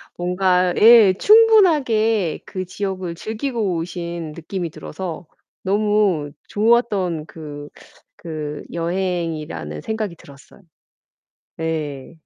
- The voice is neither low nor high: Yes, medium, 180 Hz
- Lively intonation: No, average, 4.6 semitones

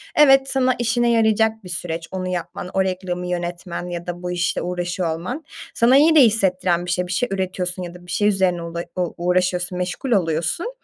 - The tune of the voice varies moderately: Yes, average, 3.9 semitones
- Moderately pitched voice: Yes, medium, 180 Hz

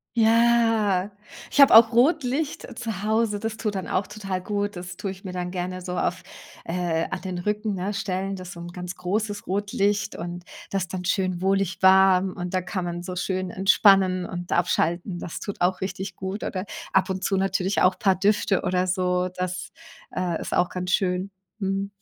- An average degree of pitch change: No, narrow, 2.1 semitones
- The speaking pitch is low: No, high, 190 Hz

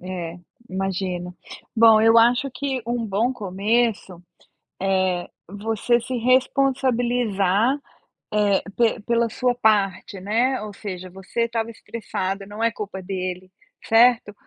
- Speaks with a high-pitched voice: Yes, high, 215 Hz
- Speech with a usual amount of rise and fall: Yes, average, 3.7 semitones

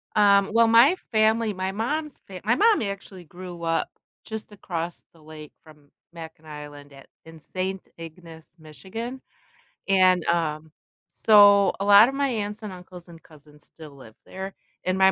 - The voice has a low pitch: No, medium, 185 Hz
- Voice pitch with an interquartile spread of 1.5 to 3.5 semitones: No, average, 4.6 semitones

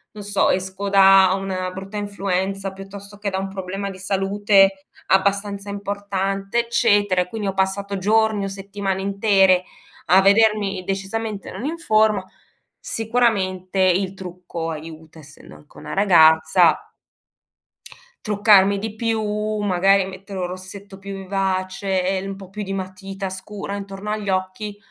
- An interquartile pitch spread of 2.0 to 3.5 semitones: No, narrow, 1.3 semitones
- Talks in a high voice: Yes, high, 195 Hz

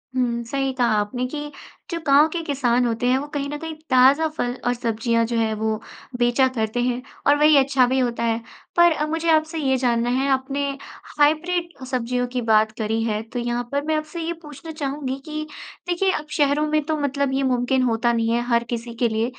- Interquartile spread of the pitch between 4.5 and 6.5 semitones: No, average, 3.8 semitones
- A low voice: No, very high, 260 Hz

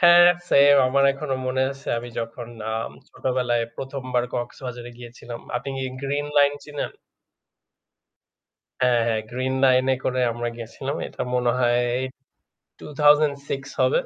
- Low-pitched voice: Yes, low, 130 Hz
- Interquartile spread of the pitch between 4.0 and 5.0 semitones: No, average, 2.7 semitones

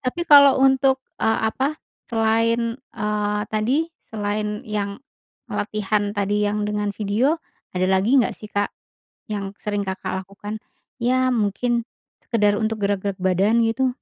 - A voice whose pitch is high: Yes, high, 215 Hz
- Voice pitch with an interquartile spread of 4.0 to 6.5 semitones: No, average, 2.8 semitones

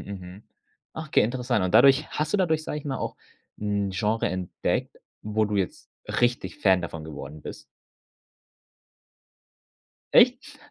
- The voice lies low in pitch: Yes, low, 105 Hz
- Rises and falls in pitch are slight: No, wide, 6.2 semitones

